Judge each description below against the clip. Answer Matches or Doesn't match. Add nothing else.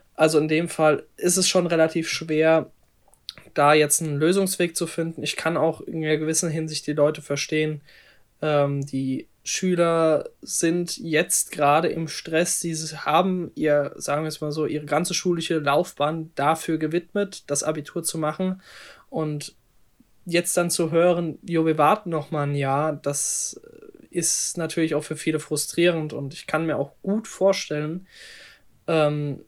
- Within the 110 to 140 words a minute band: Doesn't match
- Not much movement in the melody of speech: Matches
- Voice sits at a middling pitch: Matches